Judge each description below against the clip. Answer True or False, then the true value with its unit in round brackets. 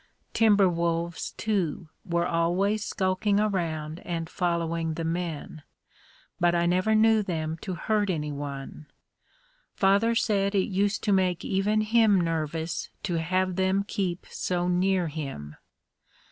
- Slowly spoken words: True (130 wpm)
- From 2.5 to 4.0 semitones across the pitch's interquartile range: True (3.2 semitones)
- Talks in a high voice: False (180 Hz)